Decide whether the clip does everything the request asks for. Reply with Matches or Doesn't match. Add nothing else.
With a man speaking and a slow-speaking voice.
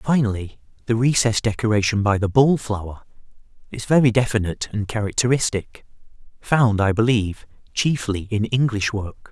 Matches